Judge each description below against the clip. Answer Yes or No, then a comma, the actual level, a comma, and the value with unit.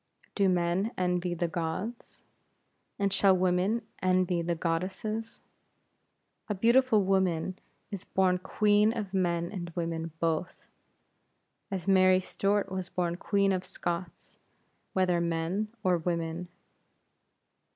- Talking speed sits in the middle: No, slow, 115 wpm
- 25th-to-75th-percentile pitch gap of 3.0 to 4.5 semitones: No, narrow, 2.4 semitones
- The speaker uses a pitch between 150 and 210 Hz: Yes, medium, 185 Hz